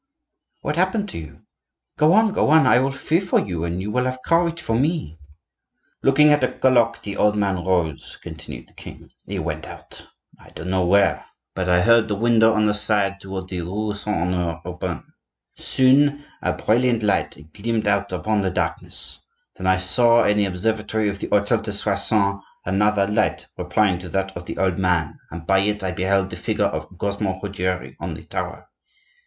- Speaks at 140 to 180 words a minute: No, average, 195 wpm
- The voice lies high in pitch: No, low, 100 Hz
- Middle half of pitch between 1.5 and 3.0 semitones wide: No, average, 3.9 semitones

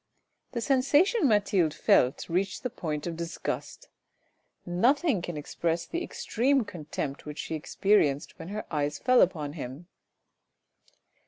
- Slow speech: Yes, slow, 130 wpm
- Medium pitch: Yes, medium, 175 Hz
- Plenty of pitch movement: Yes, wide, 8.6 semitones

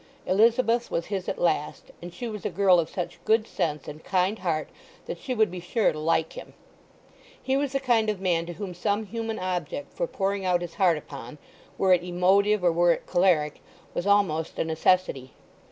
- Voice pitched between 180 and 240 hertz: Yes, medium, 185 Hz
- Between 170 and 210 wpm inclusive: Yes, average, 195 wpm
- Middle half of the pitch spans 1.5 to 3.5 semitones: No, average, 4.0 semitones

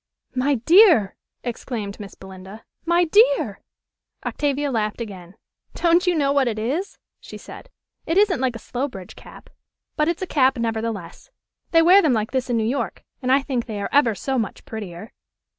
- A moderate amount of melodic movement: No, wide, 6.1 semitones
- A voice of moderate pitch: No, very high, 255 Hz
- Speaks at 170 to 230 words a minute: Yes, average, 175 wpm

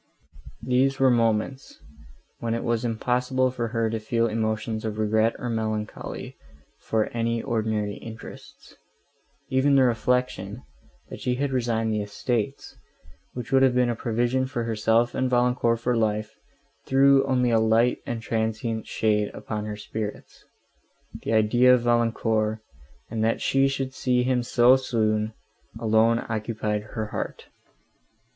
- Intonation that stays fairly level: Yes, narrow, 2.3 semitones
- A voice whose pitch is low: Yes, low, 115 Hz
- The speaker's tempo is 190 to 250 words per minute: No, average, 140 wpm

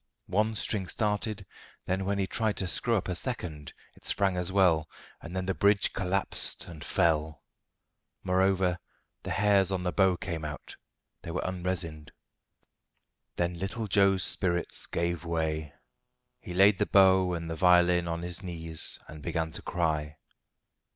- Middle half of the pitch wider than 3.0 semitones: No, narrow, 2.6 semitones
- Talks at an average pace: Yes, average, 155 wpm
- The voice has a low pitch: Yes, very low, 90 Hz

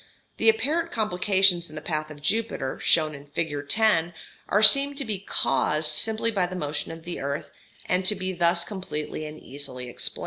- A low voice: No, medium, 170 Hz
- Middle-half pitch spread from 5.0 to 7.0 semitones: Yes, wide, 5.6 semitones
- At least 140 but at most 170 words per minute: No, average, 185 wpm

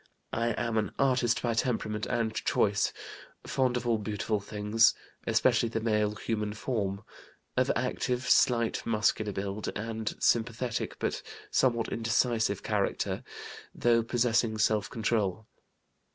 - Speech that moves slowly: Yes, slow, 125 wpm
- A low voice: Yes, low, 110 Hz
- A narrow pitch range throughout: Yes, narrow, 1.8 semitones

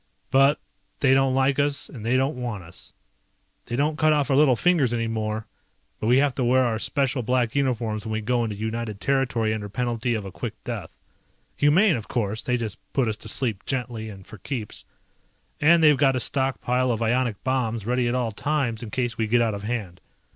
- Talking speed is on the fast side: Yes, fast, 210 wpm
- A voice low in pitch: Yes, low, 120 Hz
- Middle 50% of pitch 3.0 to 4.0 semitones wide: Yes, average, 3.3 semitones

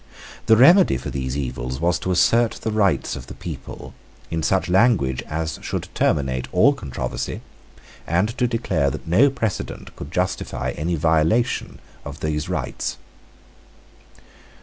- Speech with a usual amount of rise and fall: No, wide, 7.6 semitones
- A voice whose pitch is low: Yes, very low, 85 Hz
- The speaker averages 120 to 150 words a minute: Yes, average, 140 wpm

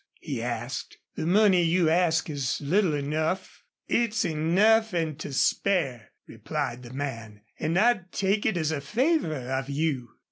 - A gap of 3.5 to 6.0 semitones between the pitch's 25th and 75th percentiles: Yes, wide, 5.4 semitones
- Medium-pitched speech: Yes, medium, 160 Hz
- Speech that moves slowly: No, average, 150 wpm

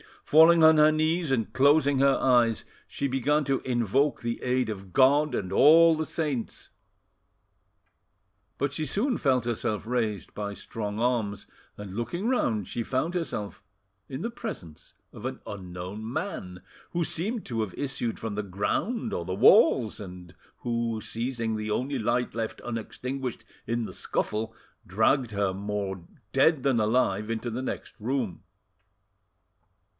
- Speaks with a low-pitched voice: Yes, low, 120 Hz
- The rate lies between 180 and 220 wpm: No, average, 150 wpm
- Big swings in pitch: No, average, 5.0 semitones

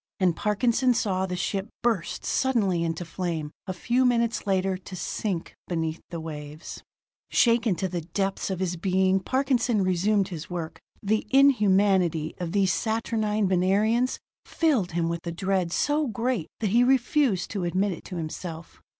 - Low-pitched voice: No, high, 190 Hz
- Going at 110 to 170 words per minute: Yes, average, 160 wpm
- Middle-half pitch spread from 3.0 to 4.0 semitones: No, average, 4.6 semitones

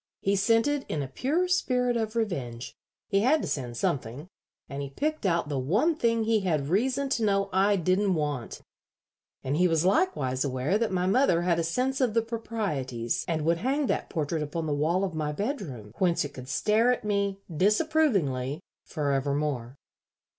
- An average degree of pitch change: No, wide, 7.9 semitones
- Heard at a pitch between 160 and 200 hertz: Yes, medium, 185 Hz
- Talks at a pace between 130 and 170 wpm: No, average, 185 wpm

